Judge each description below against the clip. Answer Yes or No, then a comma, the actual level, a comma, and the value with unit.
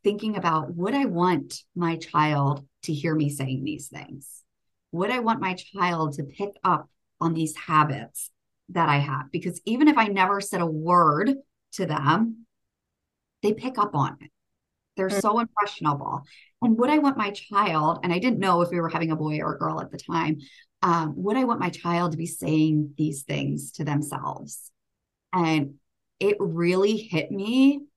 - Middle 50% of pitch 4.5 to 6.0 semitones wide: Yes, average, 5.0 semitones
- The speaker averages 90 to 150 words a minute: No, average, 180 wpm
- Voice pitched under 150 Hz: No, medium, 170 Hz